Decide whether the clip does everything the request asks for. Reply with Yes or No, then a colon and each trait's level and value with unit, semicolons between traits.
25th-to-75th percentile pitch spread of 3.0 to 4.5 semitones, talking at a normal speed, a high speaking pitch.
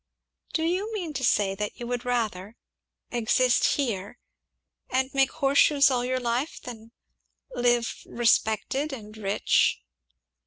No: average, 3.6 semitones; slow, 125 wpm; high, 245 Hz